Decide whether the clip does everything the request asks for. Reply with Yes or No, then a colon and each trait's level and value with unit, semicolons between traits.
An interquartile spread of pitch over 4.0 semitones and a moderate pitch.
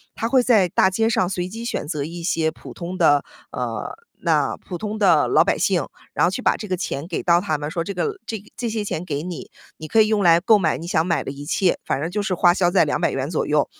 Yes: average, 4.4 semitones; medium, 180 Hz